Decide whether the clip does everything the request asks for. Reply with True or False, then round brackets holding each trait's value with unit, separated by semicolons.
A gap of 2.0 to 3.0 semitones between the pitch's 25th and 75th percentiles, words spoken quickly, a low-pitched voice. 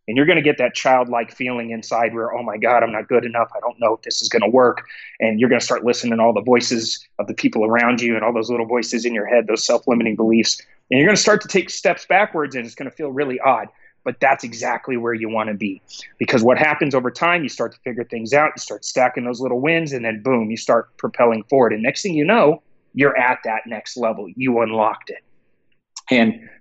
True (2.6 semitones; 255 wpm; 120 Hz)